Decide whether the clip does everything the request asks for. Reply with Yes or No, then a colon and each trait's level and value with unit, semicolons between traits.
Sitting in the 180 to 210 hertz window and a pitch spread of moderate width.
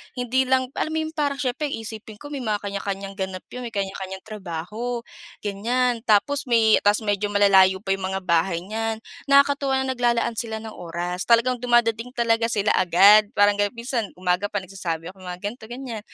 No: high, 220 Hz; average, 3.9 semitones